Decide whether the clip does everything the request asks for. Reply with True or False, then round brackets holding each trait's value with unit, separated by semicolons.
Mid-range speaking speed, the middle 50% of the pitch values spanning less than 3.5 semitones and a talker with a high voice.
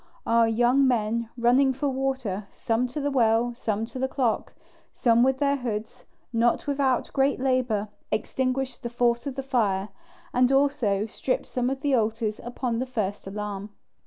True (165 wpm; 3.0 semitones; 245 Hz)